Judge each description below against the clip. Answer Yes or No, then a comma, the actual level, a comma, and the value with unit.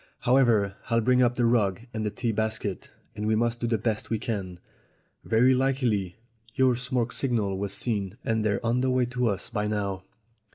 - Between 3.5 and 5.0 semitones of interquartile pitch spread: No, average, 2.9 semitones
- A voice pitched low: Yes, low, 115 Hz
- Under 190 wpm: No, average, 195 wpm